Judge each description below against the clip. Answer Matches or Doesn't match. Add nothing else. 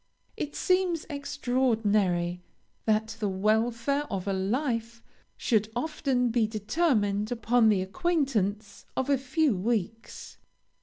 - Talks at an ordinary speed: Doesn't match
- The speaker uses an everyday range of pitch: Matches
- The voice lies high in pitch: Matches